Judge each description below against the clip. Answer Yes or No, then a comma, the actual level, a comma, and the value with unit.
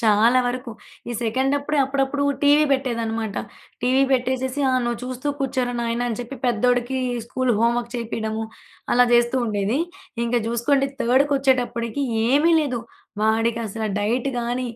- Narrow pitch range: Yes, narrow, 2.3 semitones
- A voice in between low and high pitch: No, high, 245 Hz